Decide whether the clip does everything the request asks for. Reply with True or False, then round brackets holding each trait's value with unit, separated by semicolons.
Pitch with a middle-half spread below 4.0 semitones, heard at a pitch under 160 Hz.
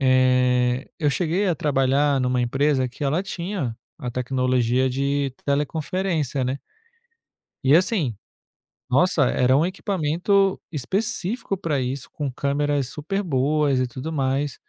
False (4.3 semitones; 140 Hz)